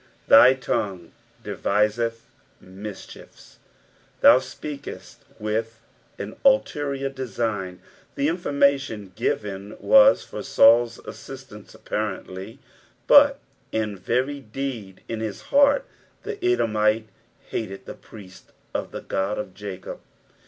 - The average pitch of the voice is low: Yes, low, 110 Hz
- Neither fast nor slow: No, slow, 105 wpm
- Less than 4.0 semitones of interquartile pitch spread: No, average, 4.9 semitones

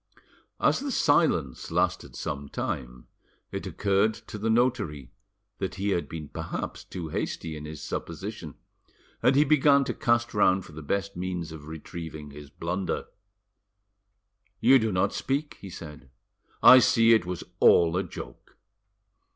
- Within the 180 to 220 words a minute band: No, average, 150 wpm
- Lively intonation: Yes, wide, 6.4 semitones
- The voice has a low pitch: Yes, very low, 95 Hz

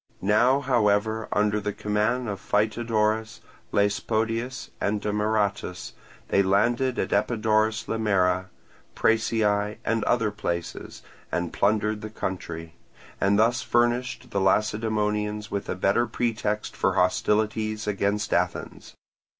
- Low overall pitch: Yes, low, 105 Hz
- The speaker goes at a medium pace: No, slow, 110 wpm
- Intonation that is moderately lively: No, narrow, 1.8 semitones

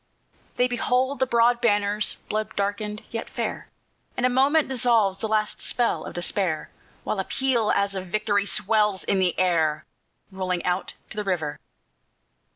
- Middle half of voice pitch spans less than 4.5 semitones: Yes, average, 3.9 semitones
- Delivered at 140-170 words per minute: Yes, average, 160 wpm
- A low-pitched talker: No, high, 210 Hz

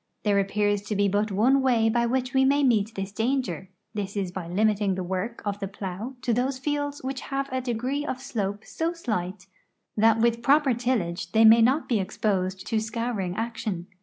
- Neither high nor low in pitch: No, high, 220 Hz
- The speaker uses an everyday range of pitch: Yes, average, 4.4 semitones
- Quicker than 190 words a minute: Yes, average, 200 wpm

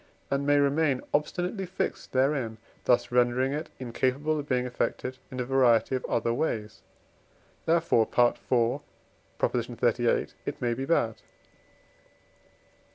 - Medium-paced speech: No, slow, 120 wpm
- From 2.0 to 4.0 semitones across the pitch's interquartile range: Yes, average, 3.2 semitones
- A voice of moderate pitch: No, low, 130 Hz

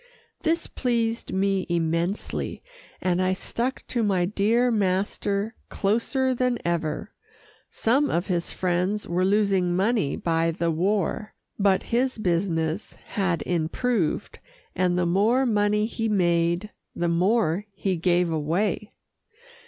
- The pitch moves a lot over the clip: No, average, 3.9 semitones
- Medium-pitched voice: No, high, 195 Hz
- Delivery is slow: Yes, slow, 120 wpm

